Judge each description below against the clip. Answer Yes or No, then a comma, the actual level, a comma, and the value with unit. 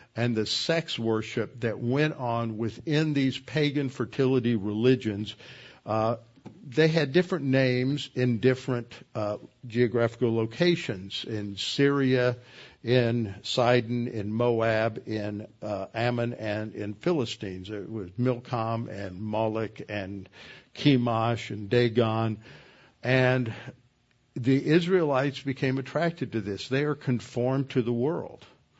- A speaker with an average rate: No, slow, 115 wpm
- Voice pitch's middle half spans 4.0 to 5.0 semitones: No, average, 3.0 semitones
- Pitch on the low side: Yes, low, 120 Hz